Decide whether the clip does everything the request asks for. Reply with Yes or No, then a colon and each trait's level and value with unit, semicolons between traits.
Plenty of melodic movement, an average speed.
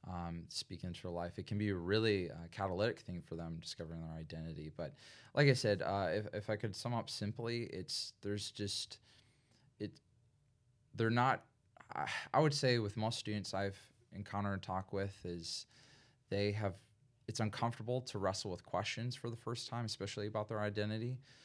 No: average, 3.6 semitones; average, 180 wpm